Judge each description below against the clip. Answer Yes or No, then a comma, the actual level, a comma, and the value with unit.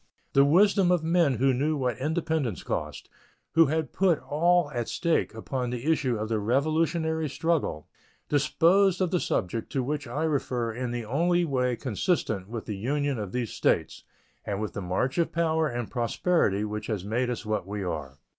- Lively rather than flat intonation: Yes, wide, 6.3 semitones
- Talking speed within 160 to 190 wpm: Yes, average, 185 wpm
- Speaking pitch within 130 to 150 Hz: Yes, low, 135 Hz